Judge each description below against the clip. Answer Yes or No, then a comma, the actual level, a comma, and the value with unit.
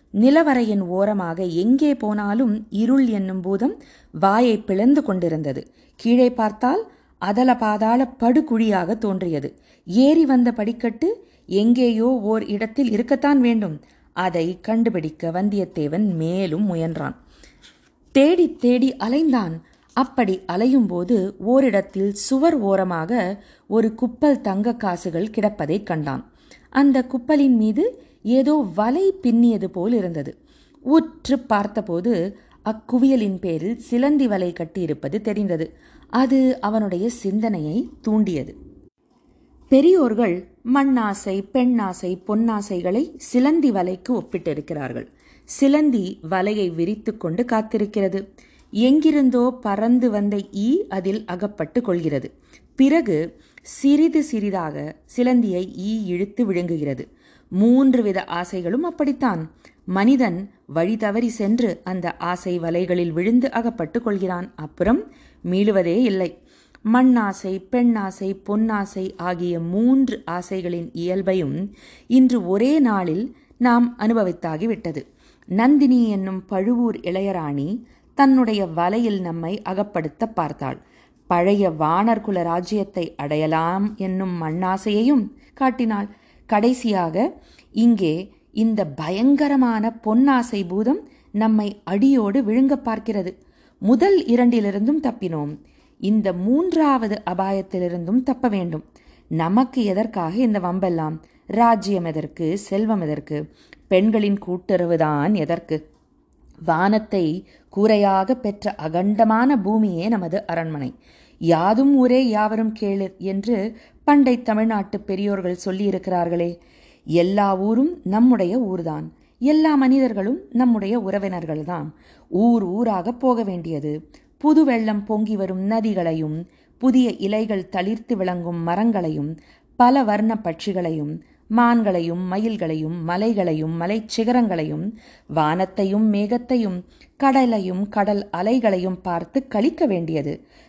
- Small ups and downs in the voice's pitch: No, average, 5.1 semitones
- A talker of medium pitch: No, high, 210 Hz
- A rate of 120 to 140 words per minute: No, average, 95 wpm